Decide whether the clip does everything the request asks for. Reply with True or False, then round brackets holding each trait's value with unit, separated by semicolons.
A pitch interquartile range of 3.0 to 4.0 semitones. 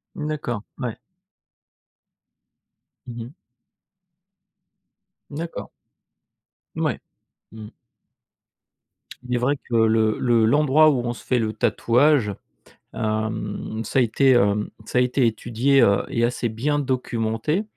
True (3.5 semitones)